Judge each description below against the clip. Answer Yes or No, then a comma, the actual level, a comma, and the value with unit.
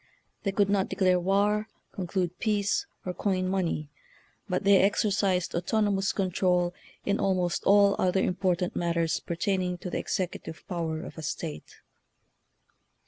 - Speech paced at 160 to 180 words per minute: No, slow, 135 wpm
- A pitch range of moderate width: No, narrow, 2.1 semitones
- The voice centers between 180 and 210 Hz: Yes, medium, 185 Hz